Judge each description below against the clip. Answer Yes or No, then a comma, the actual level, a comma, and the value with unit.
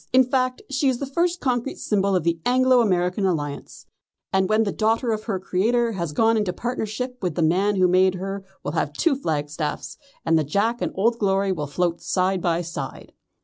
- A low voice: No, high, 195 Hz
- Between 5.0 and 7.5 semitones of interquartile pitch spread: Yes, average, 5.3 semitones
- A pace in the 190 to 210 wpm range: Yes, average, 200 wpm